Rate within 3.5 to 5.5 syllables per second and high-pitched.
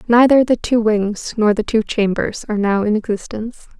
Yes: 5.2 syllables/s; high, 220 Hz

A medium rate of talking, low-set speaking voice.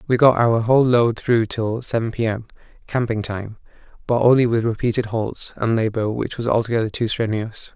Yes: average, 185 wpm; low, 115 Hz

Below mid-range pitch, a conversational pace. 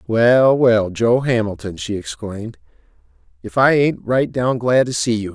Yes: low, 120 Hz; average, 170 wpm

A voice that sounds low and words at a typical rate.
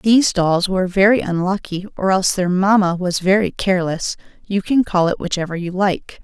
No: high, 190 Hz; average, 185 wpm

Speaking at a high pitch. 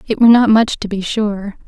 Yes: high, 215 Hz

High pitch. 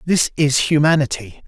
No: medium, 145 Hz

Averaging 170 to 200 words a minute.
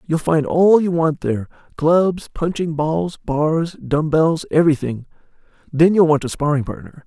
No: average, 160 wpm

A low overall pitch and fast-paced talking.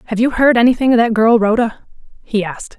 No: high, 225 Hz; fast, 215 wpm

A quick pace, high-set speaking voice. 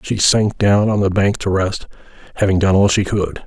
No: fast, 225 wpm; low, 100 Hz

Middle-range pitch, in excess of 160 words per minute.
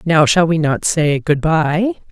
Yes: medium, 160 Hz; average, 200 wpm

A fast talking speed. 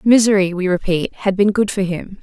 Yes: fast, 215 wpm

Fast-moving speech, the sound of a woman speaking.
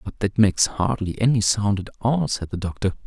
No: fast, 215 wpm; male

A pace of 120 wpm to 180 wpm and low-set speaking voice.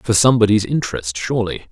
Yes: average, 140 wpm; low, 105 Hz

